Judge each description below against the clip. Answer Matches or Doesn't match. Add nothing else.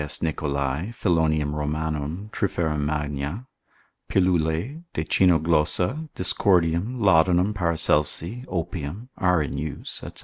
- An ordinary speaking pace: Doesn't match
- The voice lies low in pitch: Matches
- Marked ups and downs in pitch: Doesn't match